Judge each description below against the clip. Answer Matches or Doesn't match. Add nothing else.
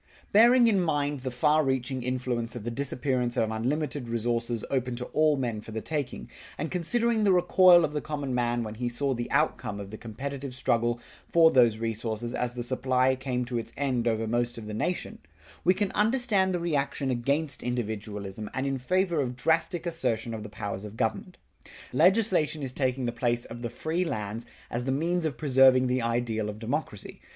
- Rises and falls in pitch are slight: Doesn't match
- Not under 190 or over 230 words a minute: Matches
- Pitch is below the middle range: Matches